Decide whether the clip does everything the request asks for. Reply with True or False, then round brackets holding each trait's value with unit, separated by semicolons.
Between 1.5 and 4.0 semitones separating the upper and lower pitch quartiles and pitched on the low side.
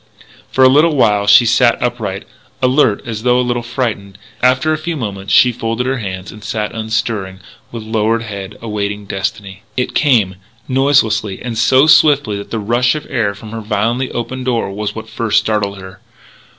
True (3.5 semitones; 115 Hz)